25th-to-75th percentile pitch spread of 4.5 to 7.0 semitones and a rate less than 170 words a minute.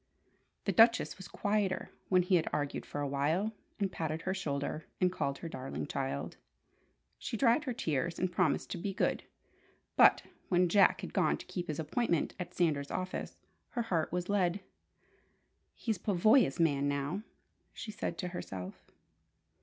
Yes: average, 5.1 semitones; average, 160 wpm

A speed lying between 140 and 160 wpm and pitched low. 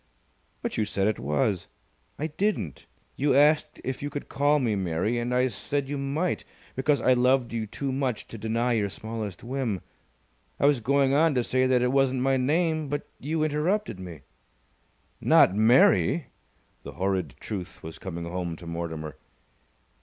No: average, 170 wpm; low, 125 Hz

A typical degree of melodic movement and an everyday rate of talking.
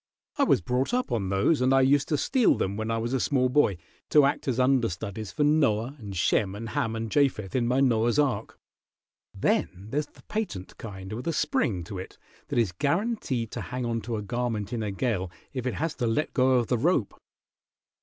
No: average, 4.4 semitones; fast, 215 wpm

